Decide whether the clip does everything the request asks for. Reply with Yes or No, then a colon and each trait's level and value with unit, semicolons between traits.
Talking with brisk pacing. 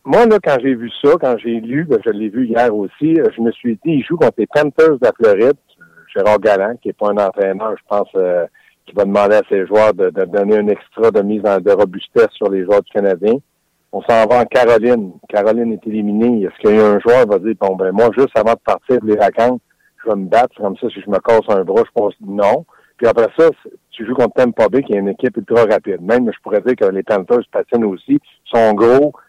Yes: fast, 255 wpm